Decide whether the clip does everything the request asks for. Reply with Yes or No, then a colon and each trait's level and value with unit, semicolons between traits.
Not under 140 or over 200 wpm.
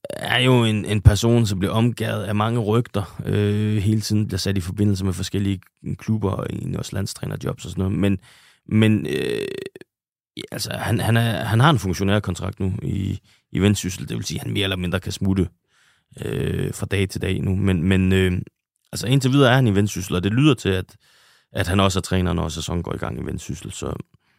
No: average, 215 wpm